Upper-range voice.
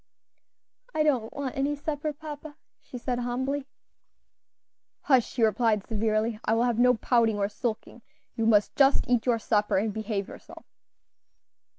Yes: high, 240 Hz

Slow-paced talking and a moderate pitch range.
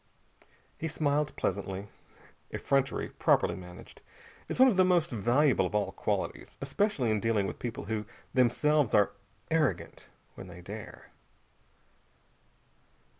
No: slow, 125 wpm; wide, 6.3 semitones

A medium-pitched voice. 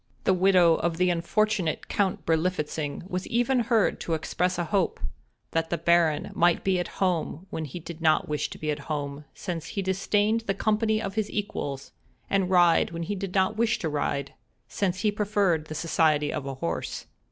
Yes: medium, 175 Hz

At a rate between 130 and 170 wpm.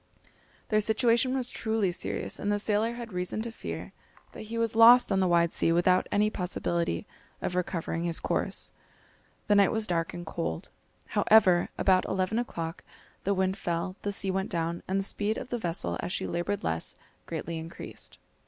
No: average, 180 wpm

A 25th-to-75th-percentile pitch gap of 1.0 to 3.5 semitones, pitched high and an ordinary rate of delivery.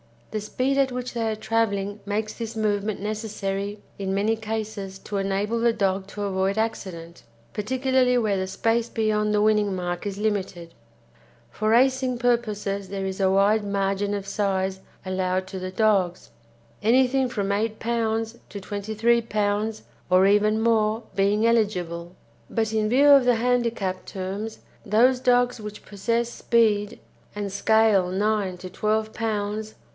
Yes: narrow, 2.5 semitones; high, 210 Hz; average, 150 wpm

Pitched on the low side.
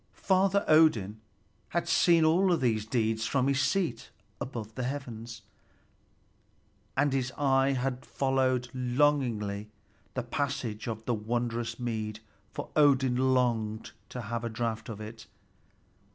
Yes: low, 125 Hz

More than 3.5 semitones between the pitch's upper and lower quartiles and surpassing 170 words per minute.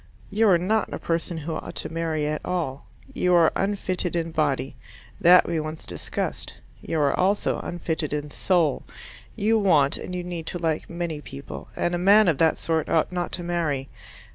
No: narrow, 2.5 semitones; average, 190 wpm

